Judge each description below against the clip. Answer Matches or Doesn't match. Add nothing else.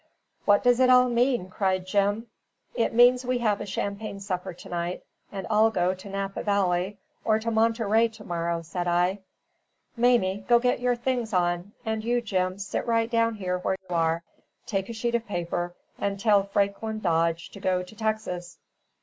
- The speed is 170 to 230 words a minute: Matches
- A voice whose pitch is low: Doesn't match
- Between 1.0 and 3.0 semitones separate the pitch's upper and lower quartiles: Doesn't match